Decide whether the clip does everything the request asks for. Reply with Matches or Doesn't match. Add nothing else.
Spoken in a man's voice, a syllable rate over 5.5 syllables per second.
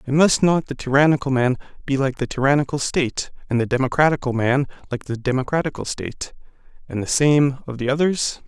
Matches